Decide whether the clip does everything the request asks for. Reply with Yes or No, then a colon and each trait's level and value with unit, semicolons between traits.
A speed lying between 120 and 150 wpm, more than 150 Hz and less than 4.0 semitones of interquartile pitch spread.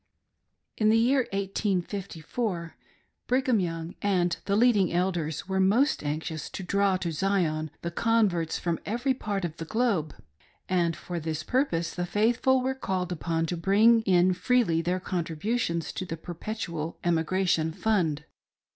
No: average, 145 wpm; medium, 185 Hz; average, 4.6 semitones